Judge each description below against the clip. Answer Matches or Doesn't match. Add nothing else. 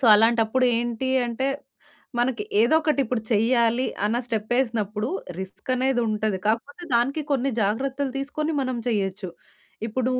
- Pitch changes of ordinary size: Matches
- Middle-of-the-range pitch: Doesn't match